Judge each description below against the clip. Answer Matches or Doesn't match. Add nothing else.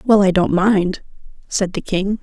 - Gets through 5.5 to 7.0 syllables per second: Doesn't match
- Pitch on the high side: Matches